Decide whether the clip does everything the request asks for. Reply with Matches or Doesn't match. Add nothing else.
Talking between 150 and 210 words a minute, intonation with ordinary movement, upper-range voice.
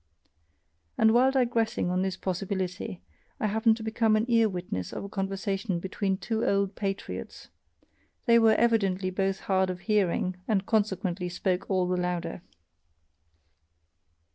Doesn't match